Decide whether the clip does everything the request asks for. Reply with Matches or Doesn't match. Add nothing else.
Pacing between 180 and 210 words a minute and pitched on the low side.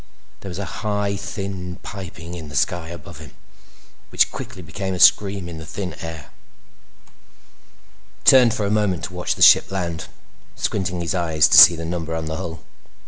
Matches